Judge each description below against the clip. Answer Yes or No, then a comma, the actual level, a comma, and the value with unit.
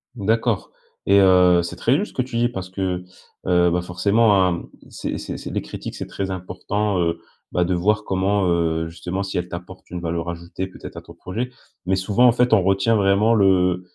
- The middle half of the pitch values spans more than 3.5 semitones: No, narrow, 2.6 semitones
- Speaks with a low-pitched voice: Yes, very low, 95 Hz